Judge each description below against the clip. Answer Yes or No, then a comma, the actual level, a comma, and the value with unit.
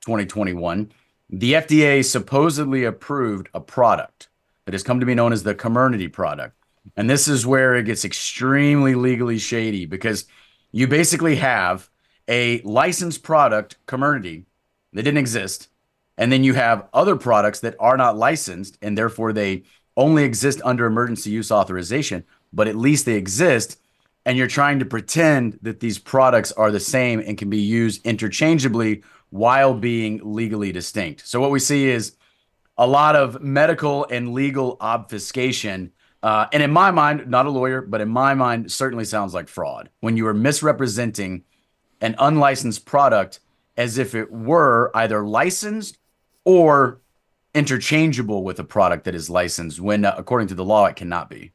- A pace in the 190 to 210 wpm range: No, average, 160 wpm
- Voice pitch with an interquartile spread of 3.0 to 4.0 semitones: No, average, 4.4 semitones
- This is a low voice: Yes, low, 120 Hz